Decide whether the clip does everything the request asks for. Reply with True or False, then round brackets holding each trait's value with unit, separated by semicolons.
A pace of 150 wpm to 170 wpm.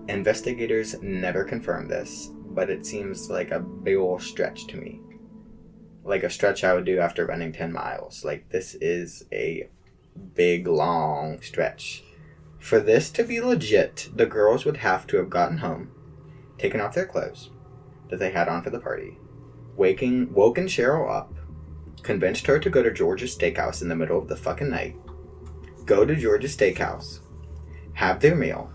True (165 wpm)